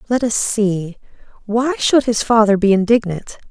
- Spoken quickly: No, average, 155 wpm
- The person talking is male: No, female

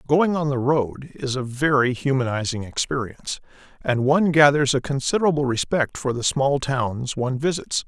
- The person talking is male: Yes, male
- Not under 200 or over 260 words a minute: No, average, 160 wpm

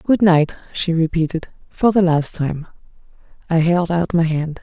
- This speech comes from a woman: Yes, female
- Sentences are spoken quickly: No, average, 170 wpm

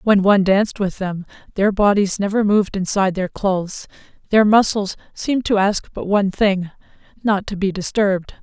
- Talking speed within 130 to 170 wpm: Yes, average, 165 wpm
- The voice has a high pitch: Yes, high, 200 Hz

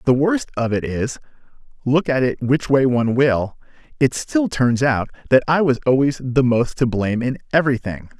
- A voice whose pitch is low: Yes, low, 130 Hz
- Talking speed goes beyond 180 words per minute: Yes, average, 190 wpm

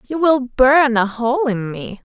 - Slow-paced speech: No, average, 200 wpm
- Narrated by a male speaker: No, female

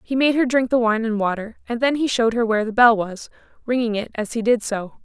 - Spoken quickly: Yes, fast, 275 wpm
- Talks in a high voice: Yes, high, 230 Hz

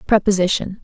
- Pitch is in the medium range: No, high, 195 Hz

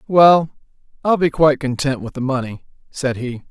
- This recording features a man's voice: Yes, male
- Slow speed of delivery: No, average, 170 wpm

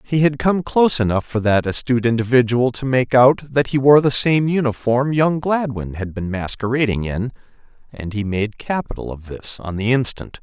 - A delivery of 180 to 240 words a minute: Yes, average, 190 wpm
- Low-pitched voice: Yes, low, 125 Hz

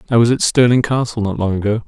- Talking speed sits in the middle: No, fast, 255 wpm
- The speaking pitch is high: No, low, 115 Hz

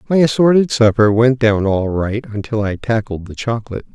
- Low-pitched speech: Yes, low, 115 Hz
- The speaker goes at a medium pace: Yes, average, 180 wpm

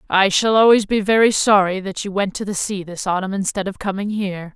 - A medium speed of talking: No, fast, 235 wpm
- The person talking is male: No, female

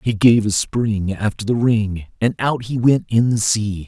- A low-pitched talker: Yes, low, 110 Hz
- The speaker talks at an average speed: No, fast, 215 wpm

